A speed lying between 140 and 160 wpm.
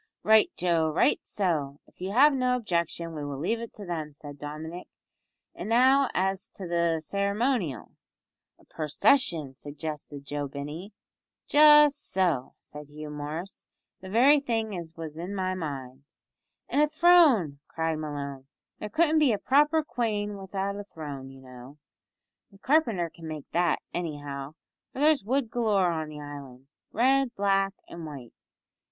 Yes: average, 155 wpm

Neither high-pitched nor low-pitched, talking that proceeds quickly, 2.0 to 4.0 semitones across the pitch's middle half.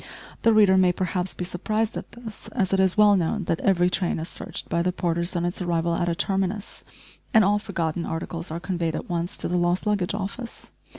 Yes: medium, 180 Hz; fast, 220 wpm; average, 2.8 semitones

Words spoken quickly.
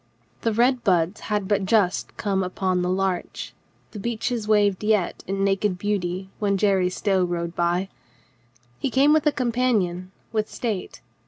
No: average, 155 wpm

